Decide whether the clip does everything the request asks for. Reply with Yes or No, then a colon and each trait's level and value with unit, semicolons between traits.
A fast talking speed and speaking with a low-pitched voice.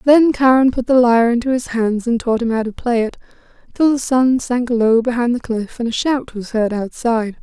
No: fast, 235 wpm; high, 240 Hz